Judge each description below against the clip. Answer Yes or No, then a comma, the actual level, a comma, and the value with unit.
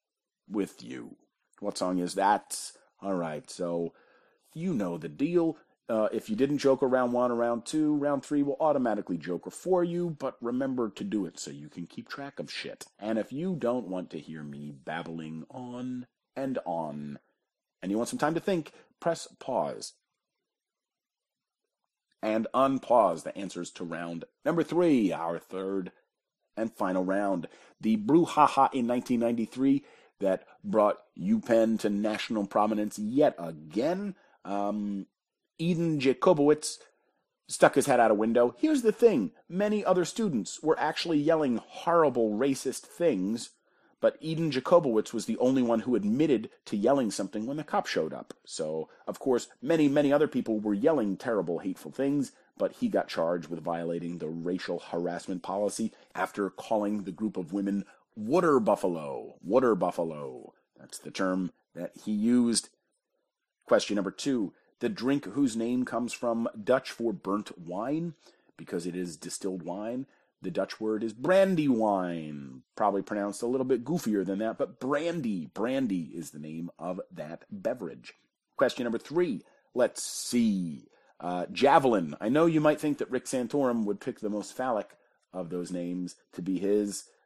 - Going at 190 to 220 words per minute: No, average, 160 wpm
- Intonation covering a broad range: Yes, wide, 7.9 semitones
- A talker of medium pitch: No, low, 115 Hz